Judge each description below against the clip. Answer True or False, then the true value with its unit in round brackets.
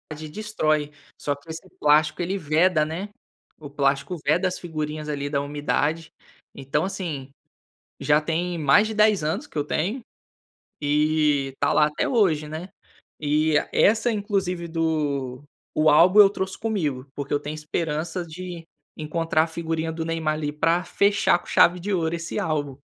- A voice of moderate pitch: True (160 Hz)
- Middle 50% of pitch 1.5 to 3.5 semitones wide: True (3.1 semitones)